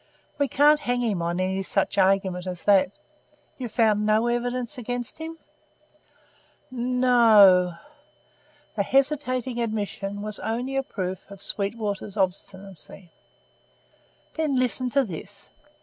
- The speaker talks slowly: Yes, slow, 120 wpm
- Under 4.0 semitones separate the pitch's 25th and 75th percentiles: No, average, 4.4 semitones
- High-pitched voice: Yes, high, 215 Hz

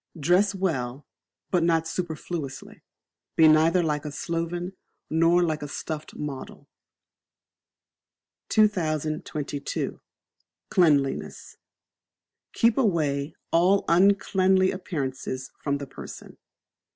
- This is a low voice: No, medium, 165 Hz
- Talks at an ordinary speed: No, slow, 90 wpm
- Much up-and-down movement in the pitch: No, average, 3.7 semitones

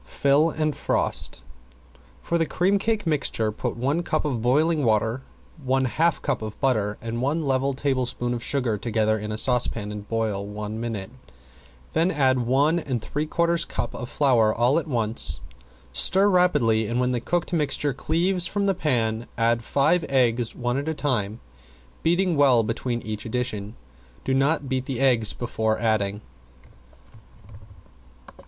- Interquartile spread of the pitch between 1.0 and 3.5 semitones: No, average, 5.1 semitones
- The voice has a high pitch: No, low, 125 Hz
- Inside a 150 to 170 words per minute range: Yes, average, 160 wpm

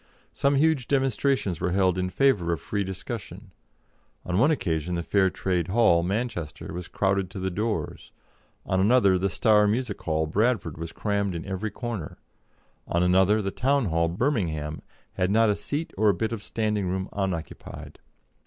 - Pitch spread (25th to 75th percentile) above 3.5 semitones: Yes, average, 4.2 semitones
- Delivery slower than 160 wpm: No, average, 170 wpm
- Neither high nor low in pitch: No, very low, 95 Hz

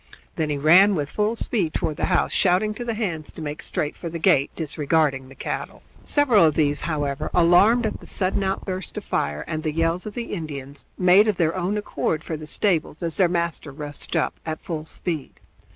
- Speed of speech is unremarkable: No, fast, 210 wpm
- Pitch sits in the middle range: Yes, medium, 165 Hz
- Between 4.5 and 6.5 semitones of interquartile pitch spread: No, average, 4.1 semitones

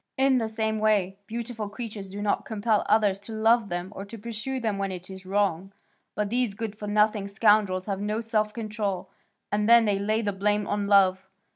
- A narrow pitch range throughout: Yes, narrow, 1.9 semitones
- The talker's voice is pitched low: No, high, 210 Hz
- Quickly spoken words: No, average, 195 wpm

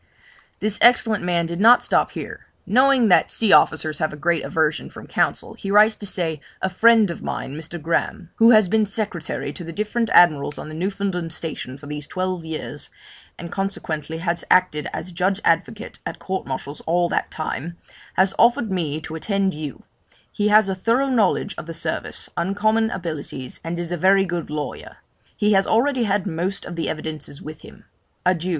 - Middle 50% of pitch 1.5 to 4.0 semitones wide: No, average, 4.5 semitones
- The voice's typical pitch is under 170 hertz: No, medium, 180 Hz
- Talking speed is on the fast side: No, average, 185 wpm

